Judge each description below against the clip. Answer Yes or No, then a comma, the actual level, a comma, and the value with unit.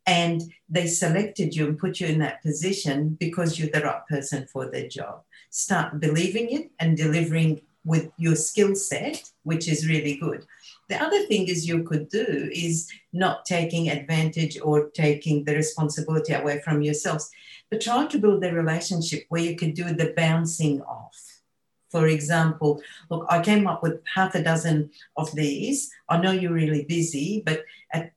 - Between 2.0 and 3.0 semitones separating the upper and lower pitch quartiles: Yes, narrow, 2.4 semitones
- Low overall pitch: No, medium, 165 Hz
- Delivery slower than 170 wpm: No, average, 175 wpm